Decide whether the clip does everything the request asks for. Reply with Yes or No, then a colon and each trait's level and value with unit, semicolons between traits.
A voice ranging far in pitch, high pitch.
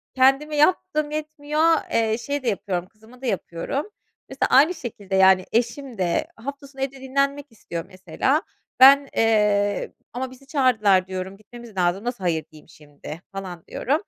Yes: wide, 6.4 semitones; high, 240 Hz